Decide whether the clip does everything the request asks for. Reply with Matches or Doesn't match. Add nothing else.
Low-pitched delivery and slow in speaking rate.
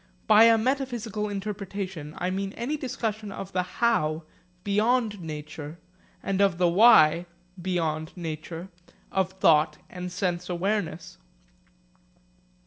Doesn't match